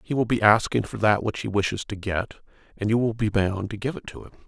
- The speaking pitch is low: Yes, low, 105 Hz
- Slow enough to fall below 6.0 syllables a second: No, 6.1 syllables/s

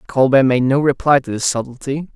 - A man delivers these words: Yes, male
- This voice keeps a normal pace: Yes, average, 195 wpm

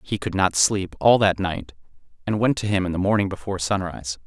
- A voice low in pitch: Yes, very low, 95 Hz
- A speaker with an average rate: No, fast, 225 wpm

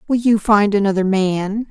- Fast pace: No, average, 175 wpm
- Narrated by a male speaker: No, female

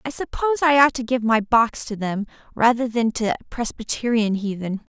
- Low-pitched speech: No, high, 235 Hz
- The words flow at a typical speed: Yes, average, 180 wpm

